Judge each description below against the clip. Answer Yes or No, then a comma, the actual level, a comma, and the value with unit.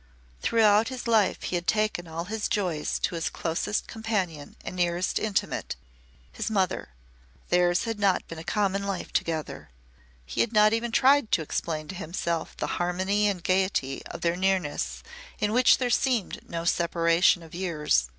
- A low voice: No, medium, 185 Hz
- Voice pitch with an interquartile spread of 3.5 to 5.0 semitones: Yes, average, 4.0 semitones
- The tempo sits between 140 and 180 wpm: Yes, average, 165 wpm